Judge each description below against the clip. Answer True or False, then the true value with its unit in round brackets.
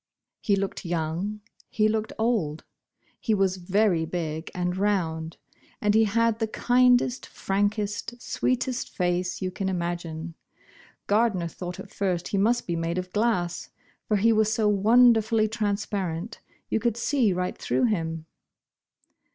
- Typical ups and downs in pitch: True (3.9 semitones)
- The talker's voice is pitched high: True (200 Hz)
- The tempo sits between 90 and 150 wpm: True (145 wpm)